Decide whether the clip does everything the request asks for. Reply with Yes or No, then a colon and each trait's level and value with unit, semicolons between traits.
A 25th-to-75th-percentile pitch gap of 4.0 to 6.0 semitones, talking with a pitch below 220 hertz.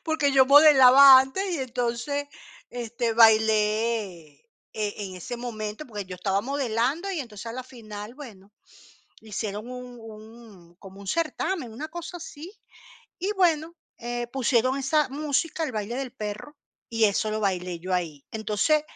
No: average, 4.8 semitones; high, 235 Hz